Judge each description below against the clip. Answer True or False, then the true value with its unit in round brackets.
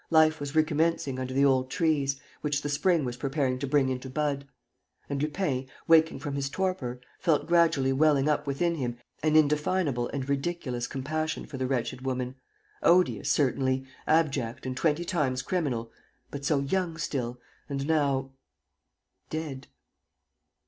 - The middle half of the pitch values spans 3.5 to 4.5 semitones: False (3.1 semitones)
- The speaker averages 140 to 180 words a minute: True (150 wpm)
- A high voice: False (140 Hz)